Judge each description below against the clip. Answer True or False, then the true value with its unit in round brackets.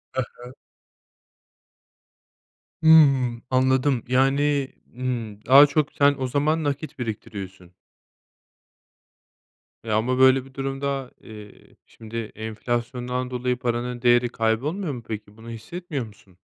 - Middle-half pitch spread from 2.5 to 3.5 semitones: True (3.1 semitones)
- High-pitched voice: False (125 Hz)